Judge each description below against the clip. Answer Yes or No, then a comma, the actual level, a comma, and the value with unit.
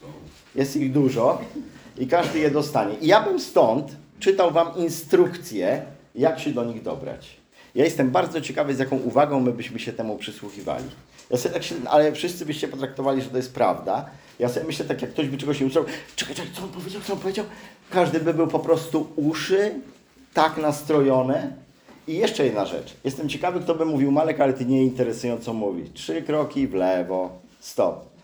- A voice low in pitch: No, medium, 150 Hz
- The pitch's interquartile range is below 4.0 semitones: No, average, 4.5 semitones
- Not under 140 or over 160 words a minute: No, average, 190 wpm